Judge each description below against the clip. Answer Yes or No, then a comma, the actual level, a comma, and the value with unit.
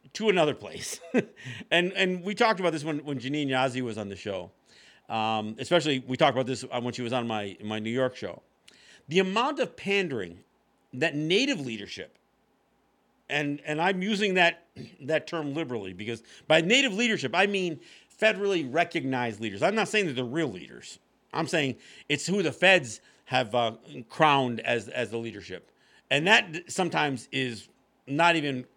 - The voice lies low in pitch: No, medium, 145 Hz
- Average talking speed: Yes, average, 170 wpm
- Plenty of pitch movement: Yes, wide, 6.7 semitones